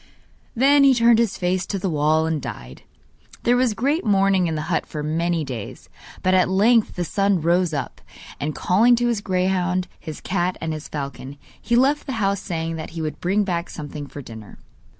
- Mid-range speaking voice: Yes, medium, 180 Hz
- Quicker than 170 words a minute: Yes, average, 200 wpm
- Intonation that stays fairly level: No, average, 5.0 semitones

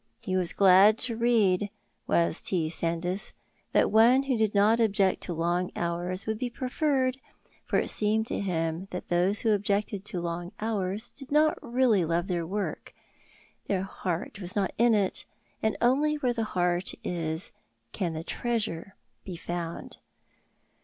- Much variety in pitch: No, average, 4.3 semitones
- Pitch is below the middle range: No, high, 195 Hz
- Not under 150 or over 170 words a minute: Yes, average, 160 wpm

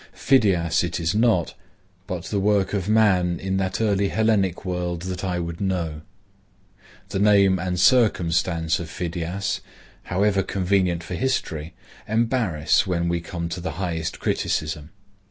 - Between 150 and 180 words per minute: No, average, 140 wpm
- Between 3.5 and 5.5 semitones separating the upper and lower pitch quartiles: No, average, 2.8 semitones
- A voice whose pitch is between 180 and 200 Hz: No, very low, 90 Hz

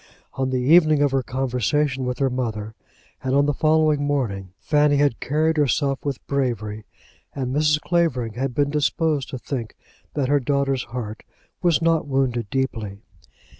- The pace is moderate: Yes, average, 160 wpm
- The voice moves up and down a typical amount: Yes, average, 3.0 semitones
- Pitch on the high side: No, low, 135 Hz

